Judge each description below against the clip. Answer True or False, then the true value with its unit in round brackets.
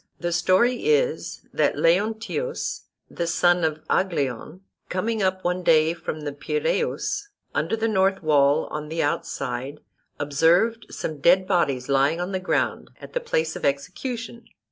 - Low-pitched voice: False (175 Hz)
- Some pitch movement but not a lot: False (6.4 semitones)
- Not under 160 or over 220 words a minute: False (145 wpm)